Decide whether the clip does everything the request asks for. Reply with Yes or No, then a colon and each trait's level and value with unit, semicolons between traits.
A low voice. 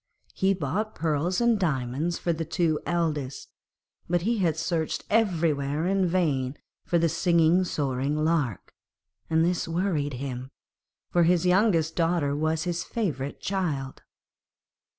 No: medium, 165 Hz